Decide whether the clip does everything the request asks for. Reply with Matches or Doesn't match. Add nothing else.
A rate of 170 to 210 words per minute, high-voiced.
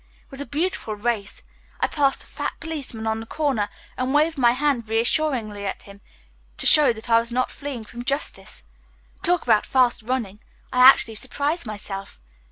Matches